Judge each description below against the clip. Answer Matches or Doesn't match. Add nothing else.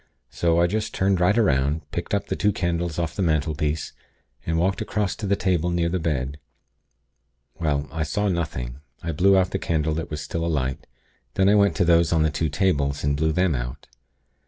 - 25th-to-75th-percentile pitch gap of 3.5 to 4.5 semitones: Matches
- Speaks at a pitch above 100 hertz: Doesn't match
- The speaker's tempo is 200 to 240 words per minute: Matches